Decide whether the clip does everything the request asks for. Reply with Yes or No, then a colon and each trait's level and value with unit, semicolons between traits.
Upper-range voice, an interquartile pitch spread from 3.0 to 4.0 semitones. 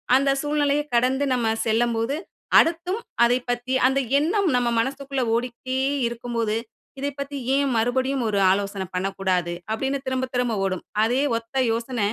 Yes: high, 245 Hz; average, 3.5 semitones